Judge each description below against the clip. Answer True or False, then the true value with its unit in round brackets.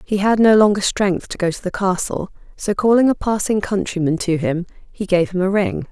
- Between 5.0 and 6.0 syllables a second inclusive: True (5.2 syllables/s)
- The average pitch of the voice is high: True (195 Hz)